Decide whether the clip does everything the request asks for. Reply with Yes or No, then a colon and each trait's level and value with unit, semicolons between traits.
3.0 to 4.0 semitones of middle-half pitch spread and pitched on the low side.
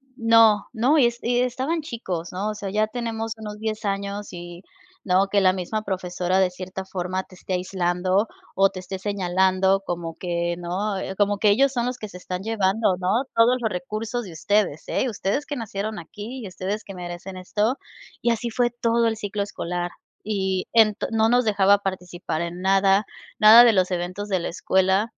No: average, 3.3 semitones; high, 200 Hz